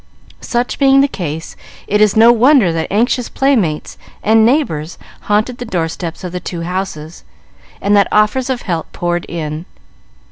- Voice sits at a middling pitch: No, high, 200 Hz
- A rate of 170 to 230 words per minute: No, average, 155 wpm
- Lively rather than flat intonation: Yes, wide, 6.2 semitones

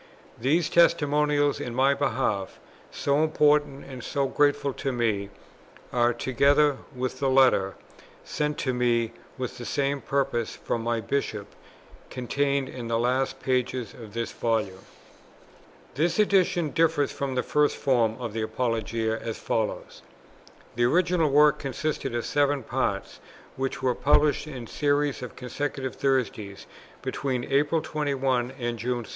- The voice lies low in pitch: Yes, low, 130 Hz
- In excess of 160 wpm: No, average, 140 wpm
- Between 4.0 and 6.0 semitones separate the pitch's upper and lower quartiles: No, average, 3.4 semitones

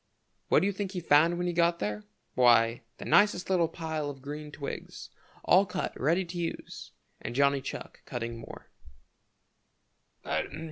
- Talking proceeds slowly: No, average, 155 wpm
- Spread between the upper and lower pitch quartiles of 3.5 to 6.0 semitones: Yes, average, 4.6 semitones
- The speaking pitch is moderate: Yes, medium, 155 Hz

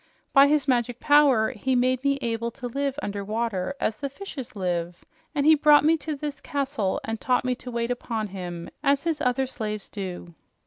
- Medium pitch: No, very high, 250 Hz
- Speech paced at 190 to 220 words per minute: Yes, average, 195 wpm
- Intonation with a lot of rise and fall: No, average, 4.7 semitones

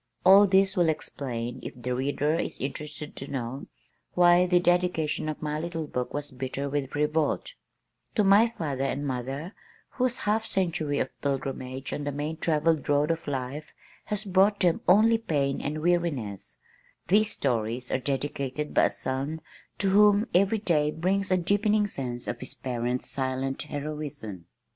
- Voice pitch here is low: No, medium, 150 Hz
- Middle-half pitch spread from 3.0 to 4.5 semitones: No, average, 5.2 semitones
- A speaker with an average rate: Yes, average, 160 wpm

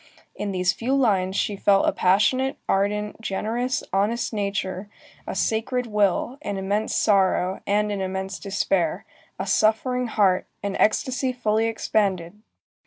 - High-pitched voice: Yes, high, 205 Hz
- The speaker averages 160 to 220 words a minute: No, slow, 135 wpm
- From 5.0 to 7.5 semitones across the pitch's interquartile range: No, average, 2.7 semitones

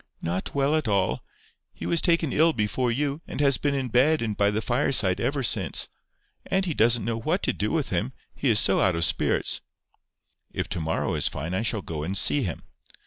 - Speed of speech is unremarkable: No, fast, 210 wpm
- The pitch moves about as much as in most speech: No, wide, 6.6 semitones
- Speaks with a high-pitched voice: No, low, 115 Hz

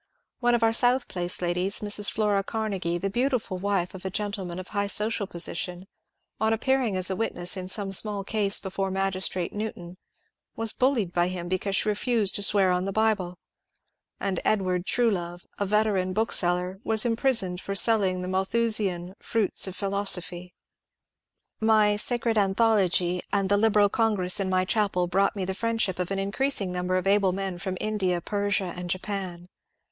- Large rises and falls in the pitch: No, average, 2.8 semitones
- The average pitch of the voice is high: Yes, high, 195 Hz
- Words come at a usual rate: Yes, average, 180 wpm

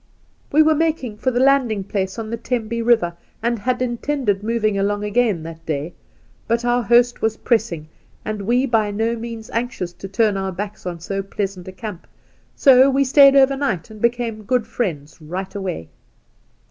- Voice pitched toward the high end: Yes, high, 220 Hz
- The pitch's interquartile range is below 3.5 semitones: No, average, 3.9 semitones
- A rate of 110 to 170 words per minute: No, average, 180 wpm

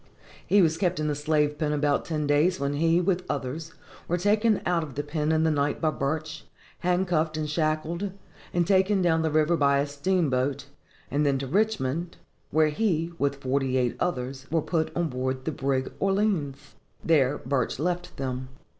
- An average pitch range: Yes, average, 3.6 semitones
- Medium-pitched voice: Yes, medium, 155 Hz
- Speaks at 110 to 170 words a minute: No, average, 180 wpm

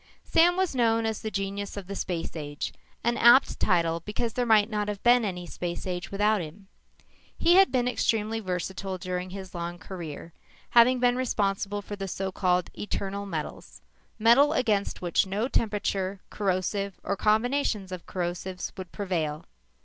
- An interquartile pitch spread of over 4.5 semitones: No, average, 3.6 semitones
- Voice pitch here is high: Yes, high, 200 Hz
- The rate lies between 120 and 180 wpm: Yes, average, 160 wpm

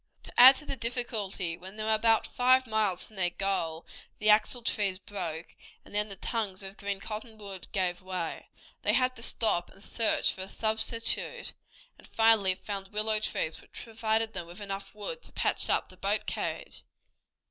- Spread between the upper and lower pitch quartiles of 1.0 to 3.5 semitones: Yes, average, 2.9 semitones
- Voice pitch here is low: No, high, 210 Hz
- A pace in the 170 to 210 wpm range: Yes, average, 180 wpm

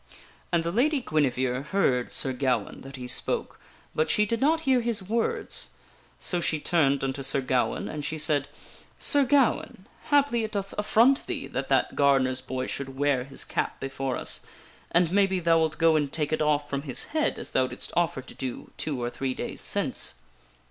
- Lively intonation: Yes, wide, 6.8 semitones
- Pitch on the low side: No, medium, 150 Hz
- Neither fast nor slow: Yes, average, 195 wpm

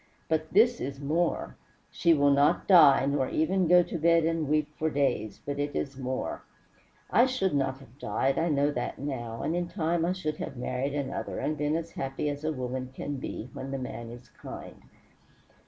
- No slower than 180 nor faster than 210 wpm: Yes, average, 200 wpm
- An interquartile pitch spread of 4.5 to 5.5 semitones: No, average, 3.4 semitones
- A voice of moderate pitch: Yes, medium, 145 Hz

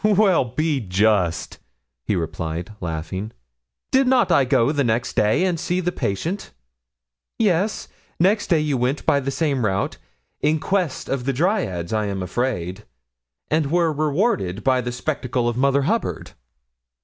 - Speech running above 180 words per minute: No, average, 150 wpm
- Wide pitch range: Yes, wide, 8.0 semitones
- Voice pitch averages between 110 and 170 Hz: Yes, low, 135 Hz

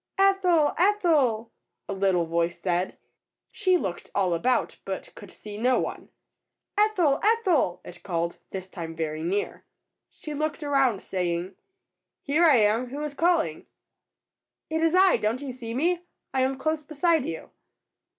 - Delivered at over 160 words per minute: No, average, 150 wpm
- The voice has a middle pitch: No, very high, 260 Hz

